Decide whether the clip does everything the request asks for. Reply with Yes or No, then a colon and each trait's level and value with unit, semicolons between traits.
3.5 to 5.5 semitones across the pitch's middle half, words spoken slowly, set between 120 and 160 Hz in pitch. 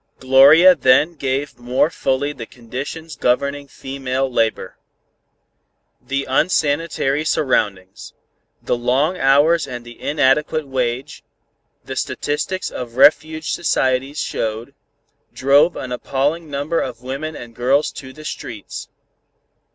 No: average, 3.1 semitones; slow, 110 wpm; low, 135 Hz